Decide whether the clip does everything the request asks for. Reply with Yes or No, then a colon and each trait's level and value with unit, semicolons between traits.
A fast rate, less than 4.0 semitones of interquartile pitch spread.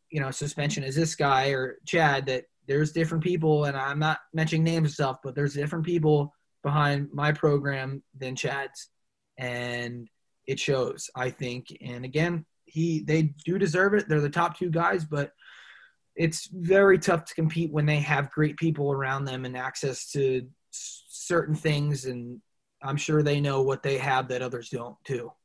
No: average, 175 wpm; average, 3.2 semitones